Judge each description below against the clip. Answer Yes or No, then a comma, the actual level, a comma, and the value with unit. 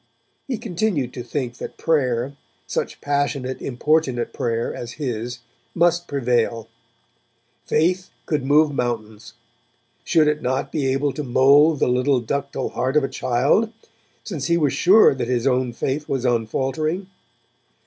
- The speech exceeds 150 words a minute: No, average, 140 wpm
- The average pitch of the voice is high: No, low, 135 Hz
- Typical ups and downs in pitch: Yes, average, 3.8 semitones